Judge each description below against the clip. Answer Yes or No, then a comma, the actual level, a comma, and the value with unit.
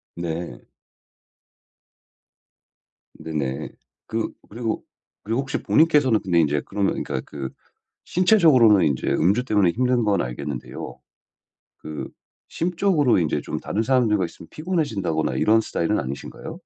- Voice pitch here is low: Yes, low, 105 Hz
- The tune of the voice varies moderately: No, wide, 8.1 semitones